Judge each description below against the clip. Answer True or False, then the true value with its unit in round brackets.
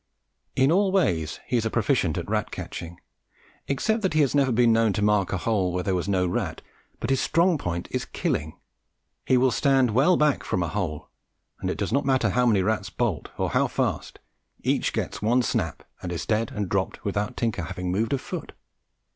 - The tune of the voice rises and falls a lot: True (6.2 semitones)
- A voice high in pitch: False (110 Hz)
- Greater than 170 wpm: True (205 wpm)